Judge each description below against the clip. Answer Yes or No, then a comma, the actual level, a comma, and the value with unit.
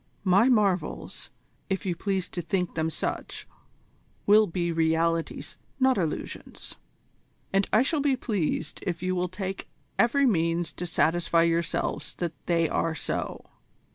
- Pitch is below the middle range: No, medium, 180 Hz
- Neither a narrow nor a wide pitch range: Yes, average, 3.3 semitones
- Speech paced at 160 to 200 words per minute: No, average, 140 wpm